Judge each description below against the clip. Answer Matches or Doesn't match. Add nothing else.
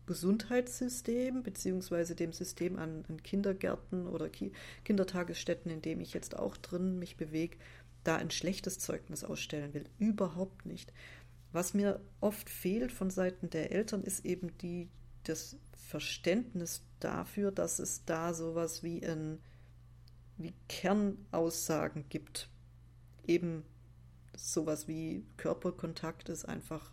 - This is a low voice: Doesn't match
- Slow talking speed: Matches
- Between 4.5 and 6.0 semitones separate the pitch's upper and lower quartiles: Doesn't match